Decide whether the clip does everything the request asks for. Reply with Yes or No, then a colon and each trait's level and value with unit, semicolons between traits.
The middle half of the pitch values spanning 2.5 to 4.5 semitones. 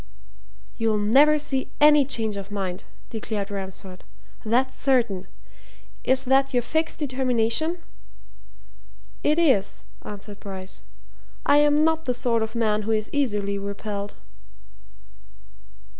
No: average, 5.2 semitones